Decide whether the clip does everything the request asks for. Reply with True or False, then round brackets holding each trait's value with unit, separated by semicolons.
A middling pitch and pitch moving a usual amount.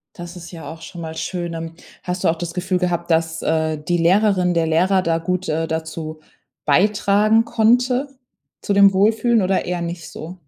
True (175 Hz; 3.2 semitones)